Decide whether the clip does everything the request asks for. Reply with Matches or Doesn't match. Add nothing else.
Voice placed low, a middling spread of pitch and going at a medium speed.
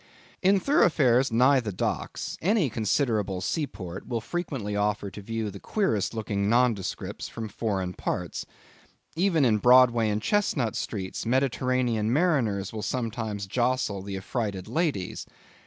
Doesn't match